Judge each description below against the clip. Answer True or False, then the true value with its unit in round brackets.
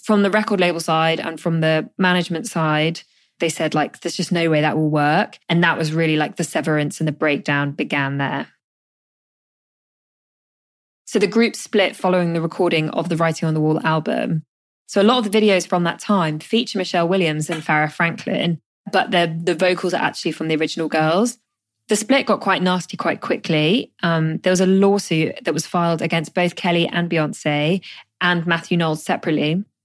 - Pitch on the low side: False (170 Hz)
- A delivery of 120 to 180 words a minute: False (190 wpm)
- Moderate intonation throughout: True (3.1 semitones)